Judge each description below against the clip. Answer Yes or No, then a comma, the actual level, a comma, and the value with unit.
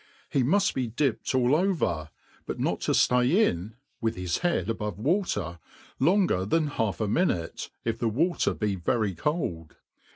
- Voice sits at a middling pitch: No, low, 115 Hz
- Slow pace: No, average, 160 wpm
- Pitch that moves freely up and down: Yes, wide, 8.3 semitones